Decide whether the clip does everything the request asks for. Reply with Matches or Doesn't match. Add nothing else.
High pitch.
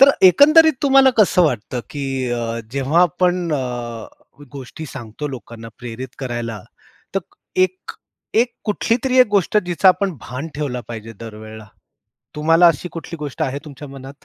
Doesn't match